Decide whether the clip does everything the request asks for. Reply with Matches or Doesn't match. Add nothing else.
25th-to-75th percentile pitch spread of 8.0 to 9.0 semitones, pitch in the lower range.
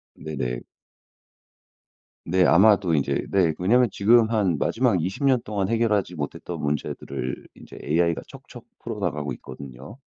Doesn't match